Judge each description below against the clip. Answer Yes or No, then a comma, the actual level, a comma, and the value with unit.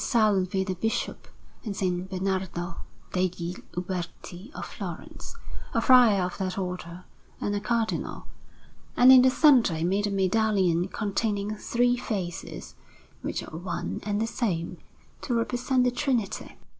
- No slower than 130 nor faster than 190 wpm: Yes, average, 140 wpm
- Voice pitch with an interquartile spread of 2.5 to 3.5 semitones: No, average, 4.1 semitones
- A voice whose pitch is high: Yes, high, 200 Hz